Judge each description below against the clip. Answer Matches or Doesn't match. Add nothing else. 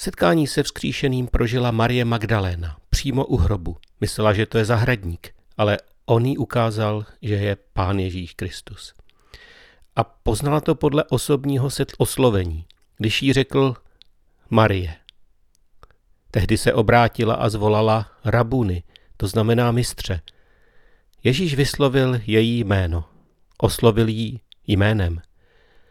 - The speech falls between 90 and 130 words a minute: Matches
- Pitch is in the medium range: Doesn't match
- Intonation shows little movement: Doesn't match